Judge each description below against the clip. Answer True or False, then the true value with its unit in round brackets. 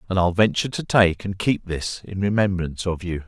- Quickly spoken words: True (220 wpm)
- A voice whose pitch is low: True (95 Hz)